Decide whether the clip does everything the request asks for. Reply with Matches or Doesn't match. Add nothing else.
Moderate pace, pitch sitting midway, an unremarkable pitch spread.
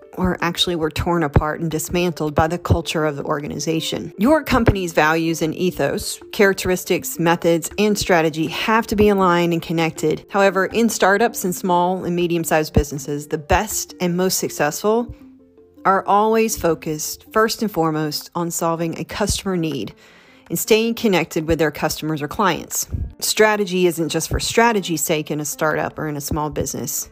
Matches